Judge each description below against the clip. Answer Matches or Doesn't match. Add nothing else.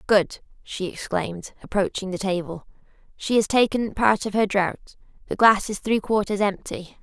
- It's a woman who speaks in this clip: Matches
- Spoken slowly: Doesn't match